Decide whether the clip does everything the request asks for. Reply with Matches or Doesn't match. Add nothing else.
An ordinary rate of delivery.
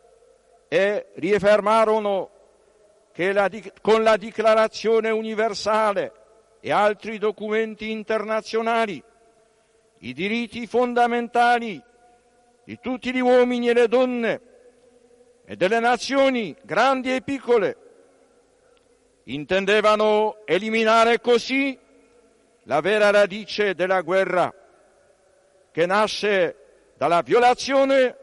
Doesn't match